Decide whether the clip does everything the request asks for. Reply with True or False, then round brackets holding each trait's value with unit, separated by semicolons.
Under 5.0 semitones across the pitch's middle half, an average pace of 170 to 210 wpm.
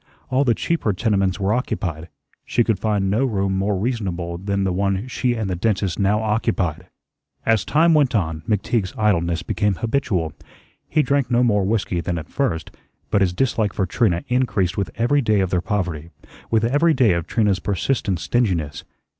True (4.2 semitones; 180 wpm)